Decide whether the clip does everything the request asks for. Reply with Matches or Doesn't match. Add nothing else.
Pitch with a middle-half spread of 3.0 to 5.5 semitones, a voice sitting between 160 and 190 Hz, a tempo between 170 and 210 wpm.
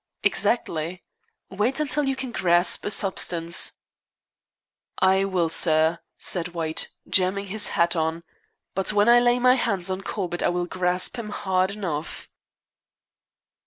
Doesn't match